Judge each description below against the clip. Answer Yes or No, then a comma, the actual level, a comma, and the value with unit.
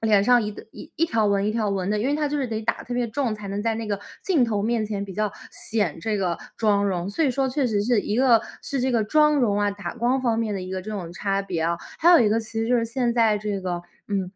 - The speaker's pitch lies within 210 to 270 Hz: Yes, high, 215 Hz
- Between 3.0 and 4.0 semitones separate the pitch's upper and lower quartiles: Yes, average, 3.3 semitones